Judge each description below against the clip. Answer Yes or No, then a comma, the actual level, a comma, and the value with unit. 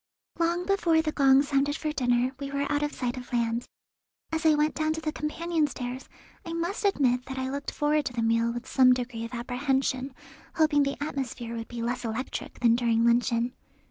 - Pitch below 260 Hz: No, very high, 265 Hz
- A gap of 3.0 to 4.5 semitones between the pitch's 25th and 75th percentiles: Yes, average, 3.9 semitones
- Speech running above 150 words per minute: Yes, average, 200 wpm